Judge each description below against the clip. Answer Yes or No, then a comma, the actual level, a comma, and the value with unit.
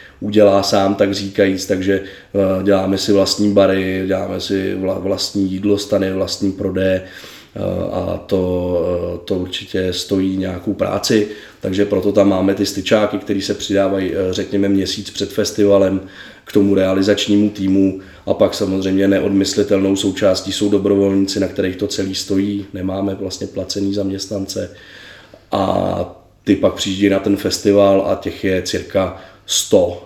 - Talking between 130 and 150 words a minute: Yes, average, 135 wpm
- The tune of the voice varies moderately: No, narrow, 1.0 semitones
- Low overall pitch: Yes, very low, 95 Hz